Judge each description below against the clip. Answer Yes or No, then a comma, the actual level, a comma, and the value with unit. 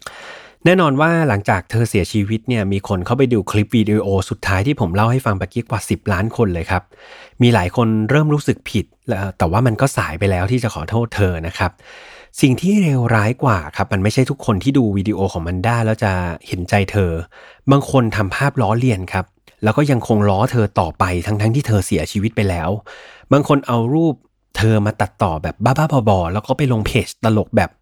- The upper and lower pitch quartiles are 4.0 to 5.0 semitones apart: Yes, average, 4.4 semitones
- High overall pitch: No, low, 110 Hz